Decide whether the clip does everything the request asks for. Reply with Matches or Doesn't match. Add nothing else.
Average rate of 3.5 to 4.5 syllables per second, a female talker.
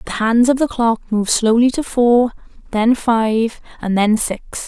Matches